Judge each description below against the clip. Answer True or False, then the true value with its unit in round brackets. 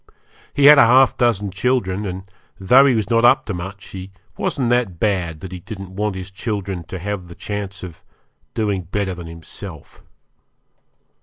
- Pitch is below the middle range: True (100 Hz)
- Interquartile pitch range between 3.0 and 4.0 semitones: True (3.4 semitones)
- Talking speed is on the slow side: False (175 wpm)